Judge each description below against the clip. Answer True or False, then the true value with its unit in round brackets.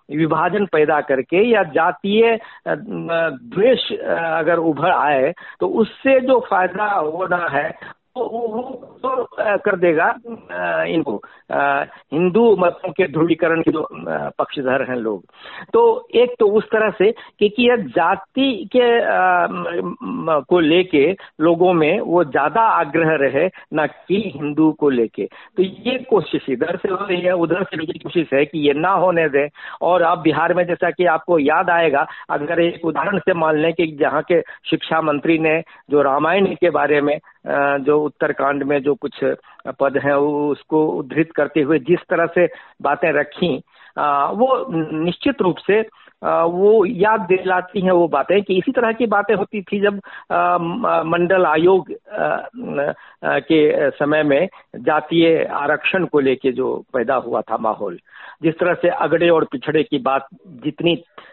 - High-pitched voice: False (170 Hz)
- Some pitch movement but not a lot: True (4.4 semitones)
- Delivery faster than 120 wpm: True (155 wpm)